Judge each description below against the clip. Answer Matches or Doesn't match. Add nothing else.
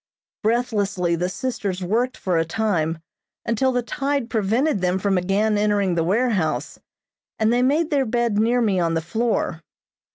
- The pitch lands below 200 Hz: Doesn't match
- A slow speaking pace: Doesn't match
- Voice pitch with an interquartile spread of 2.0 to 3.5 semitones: Doesn't match